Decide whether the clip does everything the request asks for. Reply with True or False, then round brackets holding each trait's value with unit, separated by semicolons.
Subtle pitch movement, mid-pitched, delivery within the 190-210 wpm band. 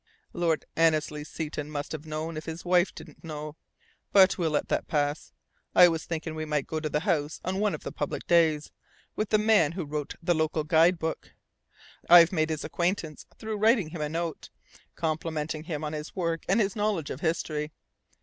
True (2.3 semitones; 160 Hz; 195 wpm)